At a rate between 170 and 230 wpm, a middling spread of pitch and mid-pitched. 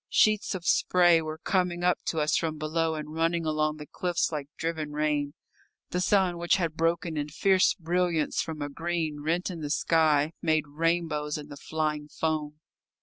No: average, 180 wpm; narrow, 2.2 semitones; medium, 160 Hz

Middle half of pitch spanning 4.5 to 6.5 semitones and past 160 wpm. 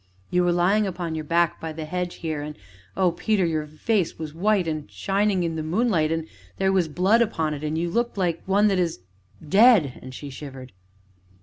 No: average, 3.8 semitones; fast, 205 wpm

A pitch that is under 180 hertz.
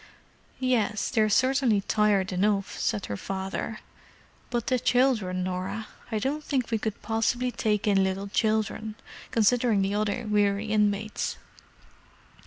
No: high, 215 Hz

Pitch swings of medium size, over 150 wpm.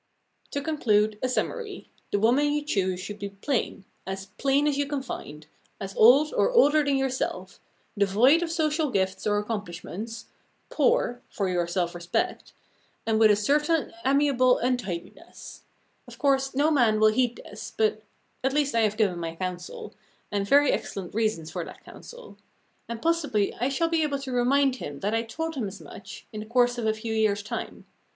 No: wide, 5.9 semitones; average, 185 wpm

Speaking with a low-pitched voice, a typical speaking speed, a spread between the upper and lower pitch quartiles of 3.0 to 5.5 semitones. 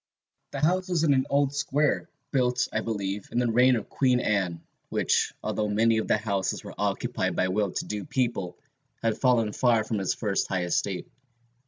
Yes: low, 115 Hz; average, 190 wpm; average, 4.3 semitones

